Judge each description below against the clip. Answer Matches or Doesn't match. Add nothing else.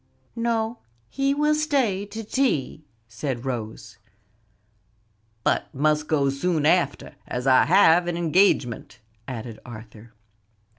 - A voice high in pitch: Doesn't match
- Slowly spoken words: Matches